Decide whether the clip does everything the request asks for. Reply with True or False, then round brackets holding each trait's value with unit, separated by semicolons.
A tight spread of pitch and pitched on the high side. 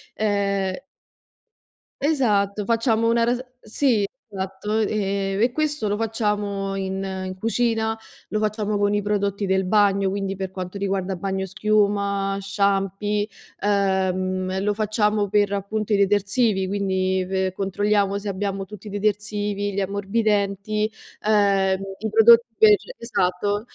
True (1.6 semitones; 200 Hz)